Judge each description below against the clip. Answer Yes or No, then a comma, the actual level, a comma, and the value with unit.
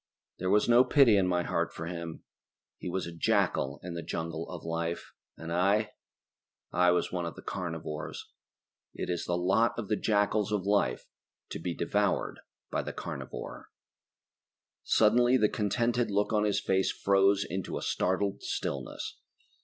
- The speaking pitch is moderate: No, very low, 95 Hz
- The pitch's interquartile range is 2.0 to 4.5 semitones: Yes, average, 3.6 semitones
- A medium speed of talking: Yes, average, 160 wpm